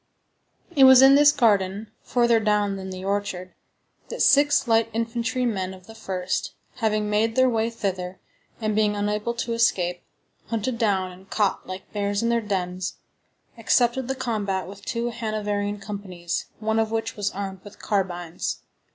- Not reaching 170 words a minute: Yes, average, 160 wpm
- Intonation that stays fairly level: No, average, 3.2 semitones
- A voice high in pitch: Yes, high, 210 Hz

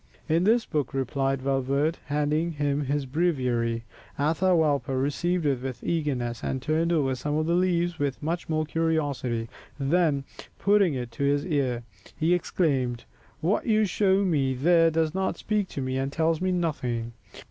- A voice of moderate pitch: Yes, medium, 150 Hz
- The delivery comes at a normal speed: Yes, average, 160 wpm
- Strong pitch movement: No, average, 4.1 semitones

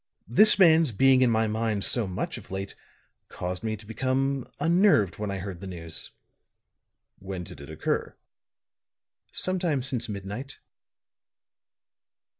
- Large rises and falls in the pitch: Yes, wide, 5.7 semitones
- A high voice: No, low, 110 Hz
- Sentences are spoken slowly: Yes, slow, 130 wpm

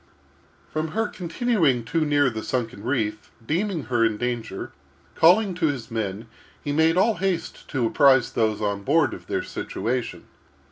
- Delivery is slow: No, average, 155 wpm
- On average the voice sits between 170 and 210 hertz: No, low, 135 Hz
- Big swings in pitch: Yes, wide, 6.6 semitones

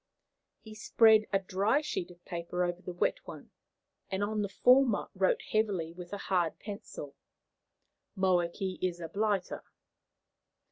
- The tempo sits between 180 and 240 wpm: No, average, 140 wpm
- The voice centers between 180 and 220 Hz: Yes, high, 190 Hz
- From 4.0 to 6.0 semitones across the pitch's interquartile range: No, average, 3.3 semitones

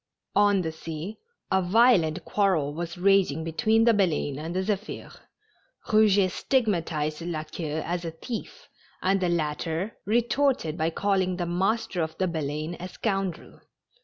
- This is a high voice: No, medium, 180 Hz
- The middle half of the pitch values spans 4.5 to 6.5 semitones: No, average, 4.0 semitones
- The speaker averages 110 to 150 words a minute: Yes, average, 145 wpm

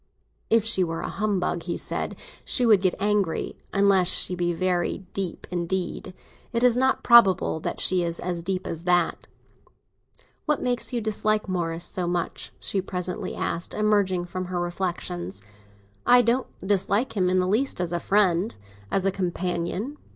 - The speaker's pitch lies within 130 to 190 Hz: Yes, medium, 185 Hz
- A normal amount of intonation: Yes, average, 3.1 semitones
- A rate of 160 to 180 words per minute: Yes, average, 165 wpm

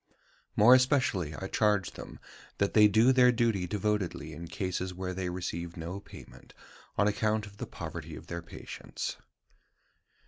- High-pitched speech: No, low, 100 Hz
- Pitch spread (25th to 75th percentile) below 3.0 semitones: No, average, 3.3 semitones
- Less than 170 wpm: Yes, average, 150 wpm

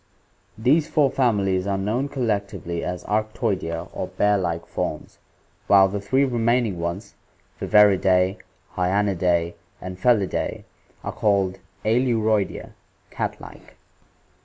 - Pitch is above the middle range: No, low, 100 Hz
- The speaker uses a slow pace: Yes, slow, 110 wpm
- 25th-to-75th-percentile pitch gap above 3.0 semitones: Yes, average, 3.5 semitones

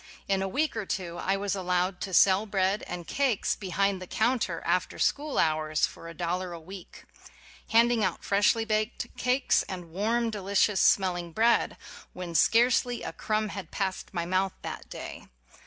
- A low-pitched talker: No, high, 195 Hz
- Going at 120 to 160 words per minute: No, average, 175 wpm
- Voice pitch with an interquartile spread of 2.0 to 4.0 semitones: Yes, average, 3.5 semitones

